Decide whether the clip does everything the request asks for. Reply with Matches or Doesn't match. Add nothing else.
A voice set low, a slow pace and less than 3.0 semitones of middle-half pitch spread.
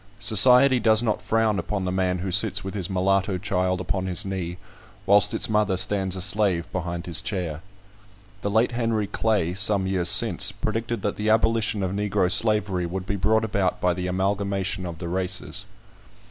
Doesn't match